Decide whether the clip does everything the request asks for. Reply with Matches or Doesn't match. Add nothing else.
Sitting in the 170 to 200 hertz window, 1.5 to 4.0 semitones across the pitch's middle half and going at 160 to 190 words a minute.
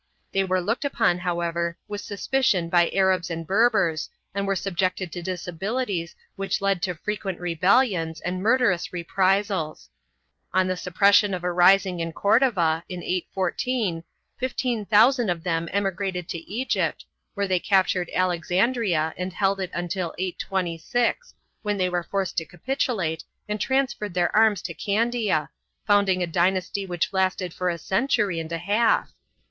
Doesn't match